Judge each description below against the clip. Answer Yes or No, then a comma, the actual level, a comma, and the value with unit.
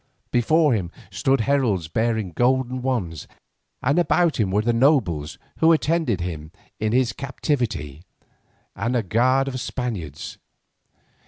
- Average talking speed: No, slow, 130 wpm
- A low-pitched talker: Yes, low, 120 Hz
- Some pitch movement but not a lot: No, wide, 6.1 semitones